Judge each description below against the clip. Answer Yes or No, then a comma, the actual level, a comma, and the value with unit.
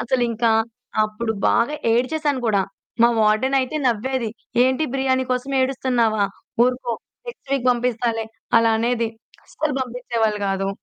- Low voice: No, high, 245 Hz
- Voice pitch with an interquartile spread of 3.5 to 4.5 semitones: No, narrow, 2.5 semitones